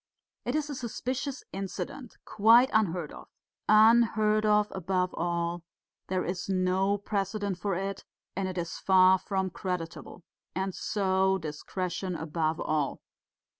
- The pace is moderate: No, slow, 130 wpm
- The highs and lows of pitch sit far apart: No, average, 2.8 semitones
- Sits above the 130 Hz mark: Yes, high, 190 Hz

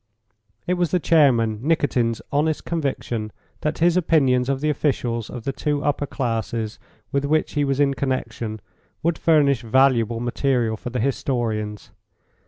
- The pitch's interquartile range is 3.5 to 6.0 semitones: Yes, average, 4.3 semitones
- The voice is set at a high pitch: No, low, 135 Hz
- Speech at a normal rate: Yes, average, 150 wpm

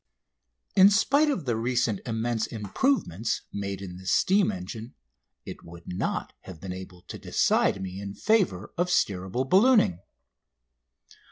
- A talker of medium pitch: No, low, 110 Hz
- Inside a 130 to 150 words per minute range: Yes, average, 140 wpm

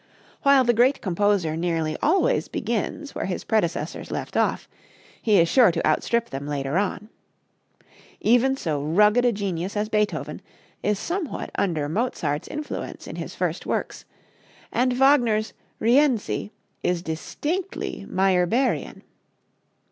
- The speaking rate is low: Yes, slow, 125 wpm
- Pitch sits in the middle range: No, high, 210 Hz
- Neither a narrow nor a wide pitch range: No, wide, 6.6 semitones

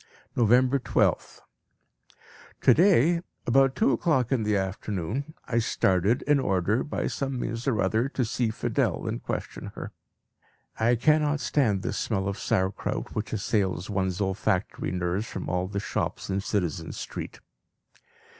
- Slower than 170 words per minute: Yes, average, 145 wpm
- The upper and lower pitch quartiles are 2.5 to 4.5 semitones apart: No, average, 5.2 semitones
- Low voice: Yes, low, 110 Hz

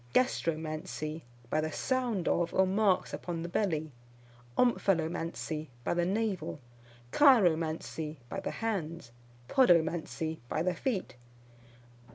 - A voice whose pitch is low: No, medium, 170 Hz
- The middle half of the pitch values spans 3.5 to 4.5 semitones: Yes, average, 4.0 semitones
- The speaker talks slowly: Yes, slow, 110 wpm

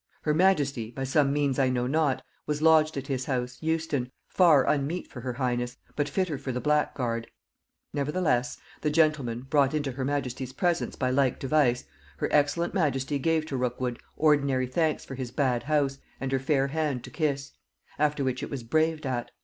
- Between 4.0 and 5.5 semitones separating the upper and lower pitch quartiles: No, average, 2.9 semitones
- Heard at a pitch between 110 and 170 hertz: Yes, medium, 140 Hz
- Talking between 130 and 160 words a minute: No, average, 185 wpm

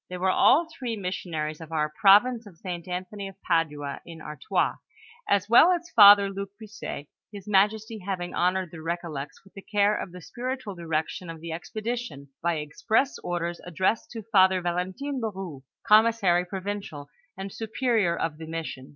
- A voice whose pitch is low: No, high, 190 Hz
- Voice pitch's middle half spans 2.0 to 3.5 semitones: No, average, 4.3 semitones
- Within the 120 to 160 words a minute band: No, average, 170 wpm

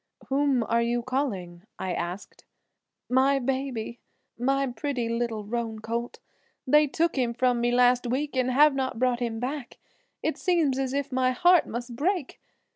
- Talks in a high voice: Yes, very high, 255 Hz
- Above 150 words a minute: Yes, average, 160 wpm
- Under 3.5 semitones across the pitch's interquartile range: Yes, narrow, 2.6 semitones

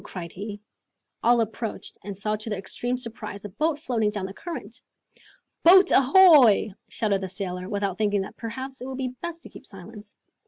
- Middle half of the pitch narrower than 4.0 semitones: No, average, 4.3 semitones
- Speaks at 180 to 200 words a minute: Yes, average, 185 wpm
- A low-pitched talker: No, high, 215 Hz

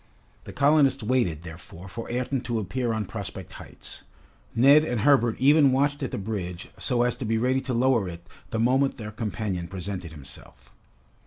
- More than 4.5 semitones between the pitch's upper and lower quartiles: Yes, wide, 5.5 semitones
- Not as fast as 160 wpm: No, average, 175 wpm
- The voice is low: Yes, low, 115 Hz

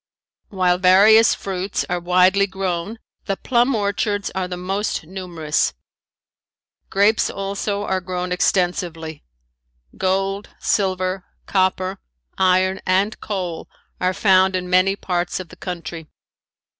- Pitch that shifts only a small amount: Yes, narrow, 1.6 semitones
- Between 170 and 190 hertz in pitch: Yes, medium, 185 Hz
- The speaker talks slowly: Yes, slow, 115 wpm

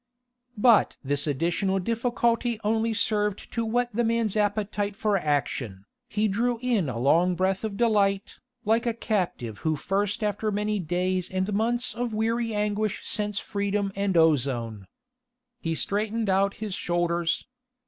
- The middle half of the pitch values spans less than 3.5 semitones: No, average, 3.8 semitones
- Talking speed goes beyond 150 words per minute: No, average, 145 wpm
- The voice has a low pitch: No, high, 205 Hz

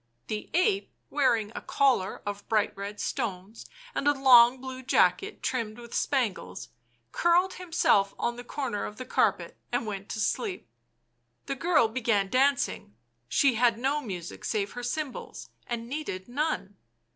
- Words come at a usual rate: Yes, average, 150 wpm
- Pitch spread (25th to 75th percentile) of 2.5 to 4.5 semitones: No, average, 5.0 semitones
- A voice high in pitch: Yes, high, 240 Hz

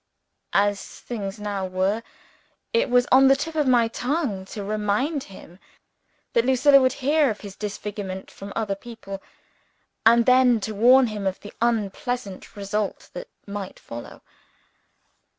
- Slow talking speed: No, average, 145 wpm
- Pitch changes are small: No, average, 4.4 semitones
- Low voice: No, high, 220 Hz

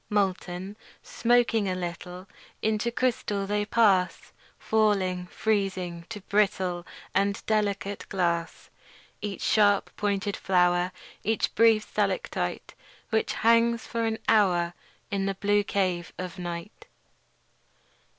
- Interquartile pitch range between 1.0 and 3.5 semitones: Yes, average, 2.9 semitones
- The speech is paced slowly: Yes, slow, 115 wpm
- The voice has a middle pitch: No, high, 200 Hz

